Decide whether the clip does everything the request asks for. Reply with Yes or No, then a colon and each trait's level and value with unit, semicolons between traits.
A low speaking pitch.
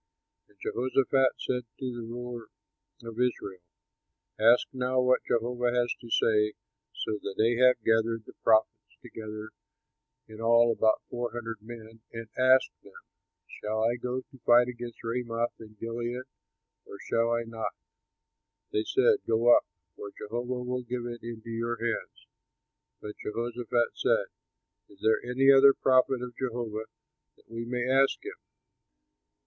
Yes: low, 120 Hz